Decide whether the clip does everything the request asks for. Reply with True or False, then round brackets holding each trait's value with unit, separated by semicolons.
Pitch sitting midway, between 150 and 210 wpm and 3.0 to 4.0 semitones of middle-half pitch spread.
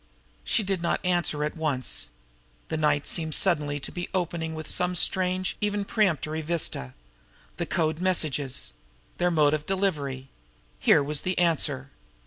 False (160 Hz; 140 wpm; 3.5 semitones)